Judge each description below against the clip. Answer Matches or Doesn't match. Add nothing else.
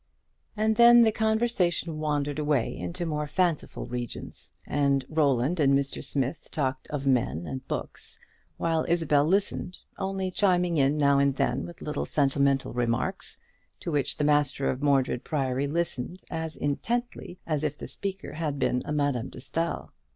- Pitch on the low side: Doesn't match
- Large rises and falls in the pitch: Doesn't match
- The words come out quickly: Doesn't match